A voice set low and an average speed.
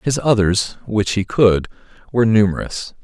No: low, 105 Hz; slow, 100 wpm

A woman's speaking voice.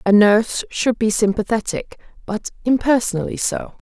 Yes: female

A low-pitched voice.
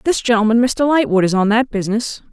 No: high, 230 Hz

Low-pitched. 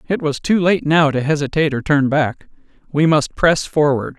No: medium, 150 Hz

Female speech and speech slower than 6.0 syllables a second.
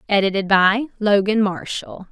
Yes: female; 4.5 syllables/s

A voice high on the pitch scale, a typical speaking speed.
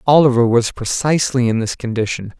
No: low, 125 Hz; average, 150 wpm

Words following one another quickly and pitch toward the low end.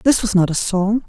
No: fast, 280 wpm; high, 205 Hz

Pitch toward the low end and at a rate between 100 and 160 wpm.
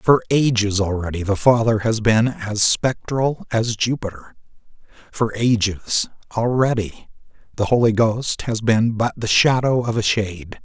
Yes: low, 110 Hz; average, 140 wpm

